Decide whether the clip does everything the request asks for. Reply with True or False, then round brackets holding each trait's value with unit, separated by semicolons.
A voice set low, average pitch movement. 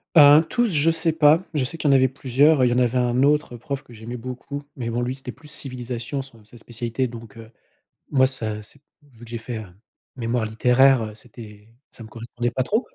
True (125 Hz; 3.2 semitones)